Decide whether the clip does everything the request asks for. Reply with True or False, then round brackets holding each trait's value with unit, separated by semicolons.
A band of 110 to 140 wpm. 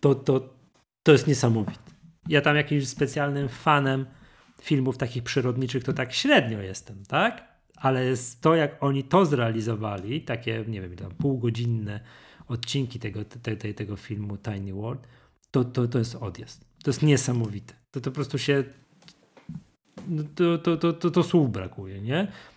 False (155 wpm)